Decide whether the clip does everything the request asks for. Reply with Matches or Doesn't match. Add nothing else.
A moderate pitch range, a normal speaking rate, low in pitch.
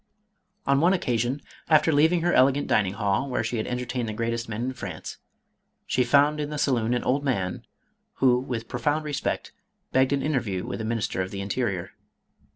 Matches